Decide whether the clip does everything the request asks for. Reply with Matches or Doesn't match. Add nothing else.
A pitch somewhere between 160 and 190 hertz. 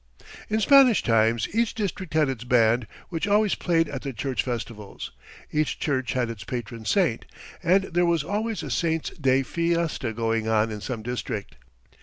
Doesn't match